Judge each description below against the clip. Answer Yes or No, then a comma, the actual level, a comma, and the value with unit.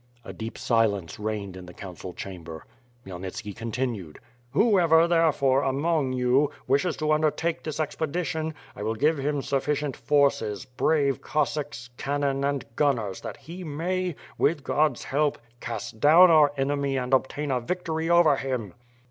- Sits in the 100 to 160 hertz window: Yes, medium, 140 Hz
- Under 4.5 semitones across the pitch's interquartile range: No, average, 5.2 semitones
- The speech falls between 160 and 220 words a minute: No, average, 145 wpm